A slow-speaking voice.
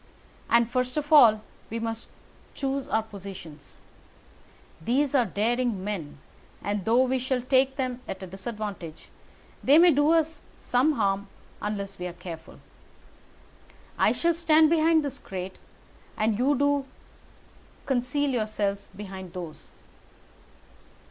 Yes: slow, 130 wpm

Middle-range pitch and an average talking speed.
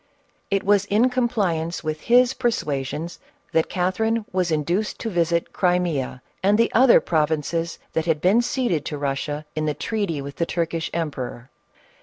Yes: medium, 170 Hz; average, 160 wpm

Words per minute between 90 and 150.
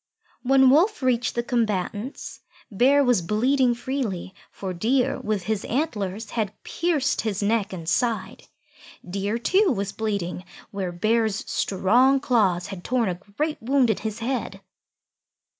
Yes: average, 140 wpm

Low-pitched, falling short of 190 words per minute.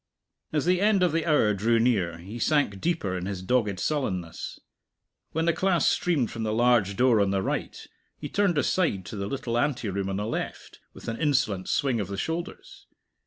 No: low, 115 Hz; average, 195 wpm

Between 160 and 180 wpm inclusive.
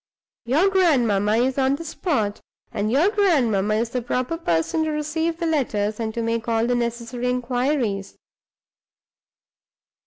No: average, 145 wpm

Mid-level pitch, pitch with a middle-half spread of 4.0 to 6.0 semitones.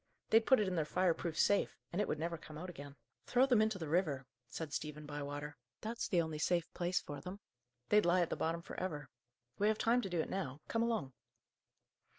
Yes: medium, 170 Hz; average, 5.1 semitones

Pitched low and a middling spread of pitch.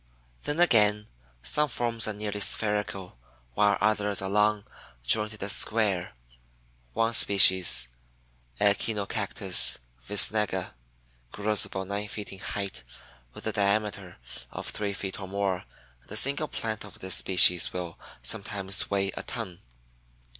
No: low, 100 Hz; narrow, 1.9 semitones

